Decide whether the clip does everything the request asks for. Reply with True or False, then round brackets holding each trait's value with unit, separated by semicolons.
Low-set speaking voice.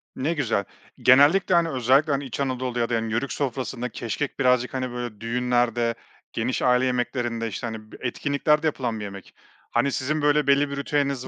True (130 Hz)